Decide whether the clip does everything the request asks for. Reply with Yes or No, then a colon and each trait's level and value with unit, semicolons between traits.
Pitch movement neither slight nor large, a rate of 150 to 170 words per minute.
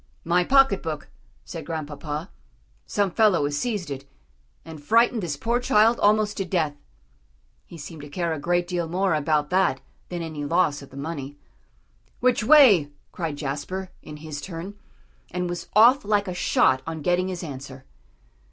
Yes: average, 4.9 semitones; average, 165 wpm